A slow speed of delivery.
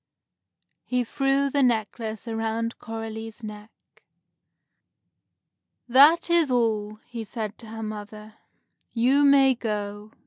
Yes: slow, 105 wpm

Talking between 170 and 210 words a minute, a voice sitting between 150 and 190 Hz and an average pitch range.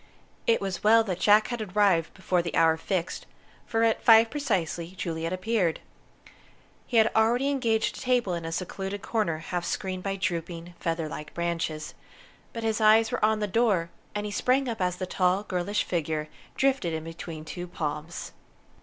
Yes: average, 175 wpm; medium, 185 Hz; average, 4.7 semitones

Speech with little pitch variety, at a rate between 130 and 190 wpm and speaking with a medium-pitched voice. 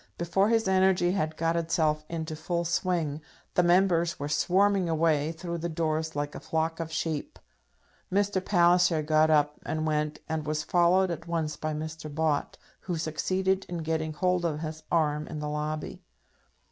Yes: narrow, 2.2 semitones; average, 170 wpm; medium, 160 Hz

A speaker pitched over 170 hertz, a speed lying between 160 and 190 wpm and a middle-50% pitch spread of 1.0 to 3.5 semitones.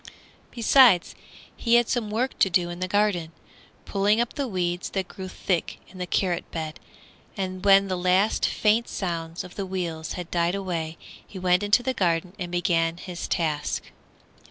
Yes: medium, 185 Hz; average, 175 wpm; average, 2.9 semitones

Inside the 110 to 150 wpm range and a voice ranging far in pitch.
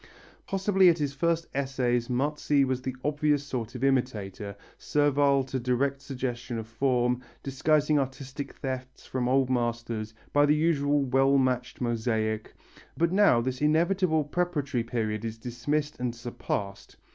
No: average, 140 wpm; average, 3.3 semitones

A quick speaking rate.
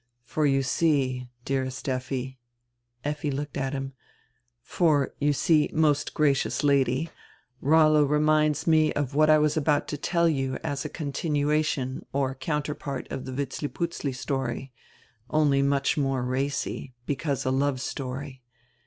No: average, 145 wpm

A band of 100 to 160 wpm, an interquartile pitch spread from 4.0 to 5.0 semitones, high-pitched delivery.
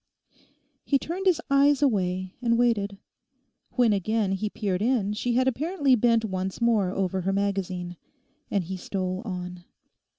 Yes: average, 145 wpm; average, 4.6 semitones; high, 205 Hz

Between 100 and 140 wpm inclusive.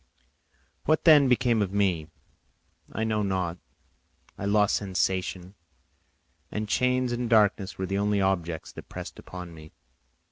Yes: slow, 135 wpm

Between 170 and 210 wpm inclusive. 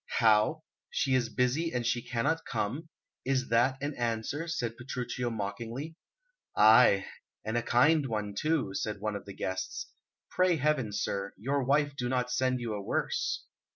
No: average, 160 wpm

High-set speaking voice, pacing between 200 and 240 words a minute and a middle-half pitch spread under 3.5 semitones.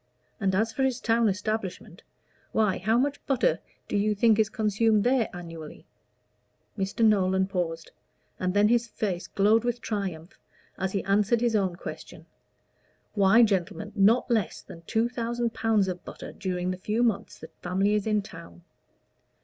No: high, 210 Hz; average, 160 wpm; average, 3.1 semitones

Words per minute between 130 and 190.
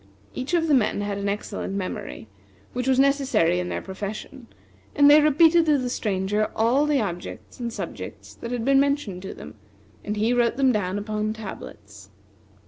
Yes: average, 180 wpm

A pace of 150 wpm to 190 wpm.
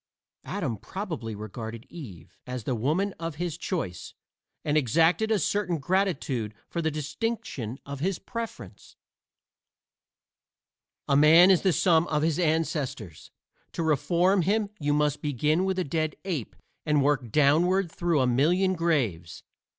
No: average, 140 wpm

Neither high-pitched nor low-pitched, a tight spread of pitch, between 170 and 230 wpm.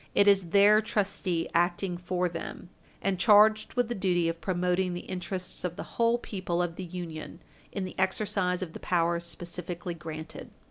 Yes: medium, 180 Hz; narrow, 2.3 semitones; average, 175 wpm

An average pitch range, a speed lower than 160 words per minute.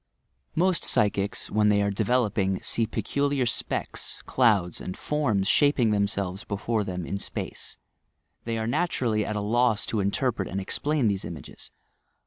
Yes: average, 3.7 semitones; average, 145 wpm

